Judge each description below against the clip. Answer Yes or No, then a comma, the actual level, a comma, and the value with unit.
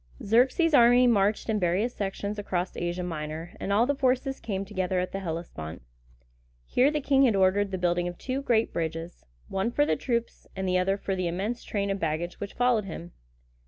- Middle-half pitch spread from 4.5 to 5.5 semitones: Yes, average, 5.1 semitones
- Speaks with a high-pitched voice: Yes, high, 195 Hz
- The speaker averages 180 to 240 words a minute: Yes, average, 195 wpm